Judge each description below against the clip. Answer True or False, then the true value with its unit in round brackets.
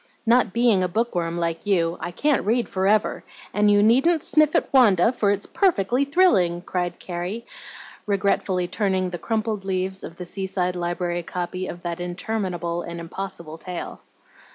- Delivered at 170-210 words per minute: False (160 wpm)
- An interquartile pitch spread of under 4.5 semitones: True (4.0 semitones)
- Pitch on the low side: False (190 Hz)